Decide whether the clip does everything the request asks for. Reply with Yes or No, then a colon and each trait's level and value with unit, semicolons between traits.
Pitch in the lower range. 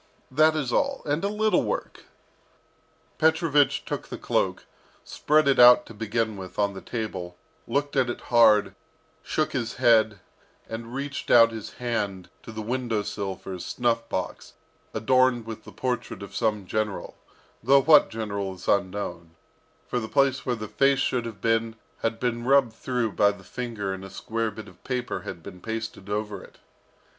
Yes: low, 115 Hz